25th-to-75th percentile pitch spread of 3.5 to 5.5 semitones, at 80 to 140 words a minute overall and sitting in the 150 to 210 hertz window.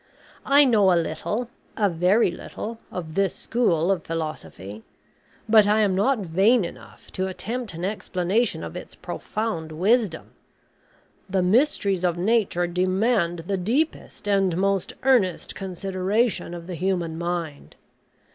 Yes: average, 4.0 semitones; slow, 135 wpm; high, 190 Hz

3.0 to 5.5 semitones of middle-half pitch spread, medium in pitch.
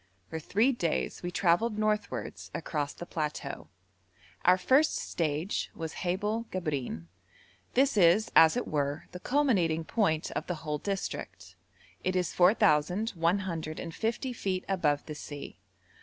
Yes: average, 5.2 semitones; medium, 175 Hz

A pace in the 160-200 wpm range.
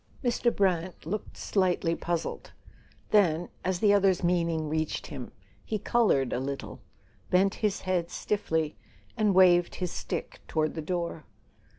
No: slow, 135 wpm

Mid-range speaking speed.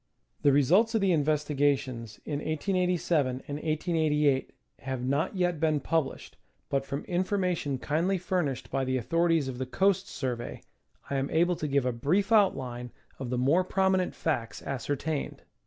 Yes: average, 155 wpm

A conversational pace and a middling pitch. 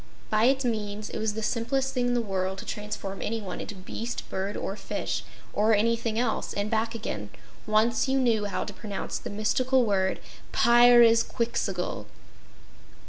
No: average, 160 wpm; high, 220 Hz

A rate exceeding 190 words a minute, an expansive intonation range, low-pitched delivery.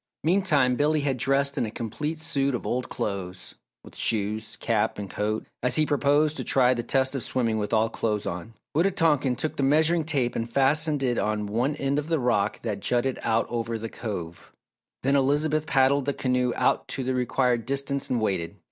No: average, 200 wpm; average, 4.1 semitones; low, 130 Hz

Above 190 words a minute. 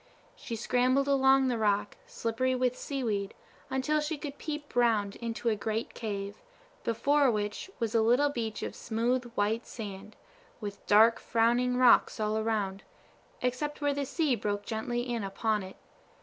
No: average, 155 wpm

